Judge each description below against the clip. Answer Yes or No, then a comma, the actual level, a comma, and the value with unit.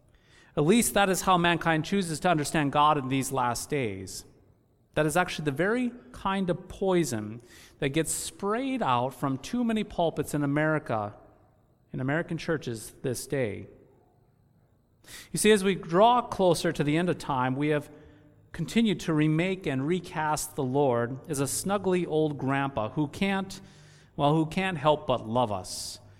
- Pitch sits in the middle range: Yes, medium, 150 Hz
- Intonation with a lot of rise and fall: Yes, wide, 5.7 semitones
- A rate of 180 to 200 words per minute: No, average, 165 wpm